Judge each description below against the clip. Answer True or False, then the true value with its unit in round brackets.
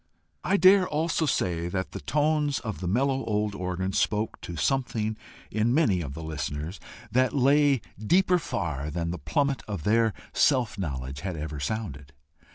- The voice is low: True (105 Hz)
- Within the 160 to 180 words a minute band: True (165 wpm)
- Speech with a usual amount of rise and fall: False (8.4 semitones)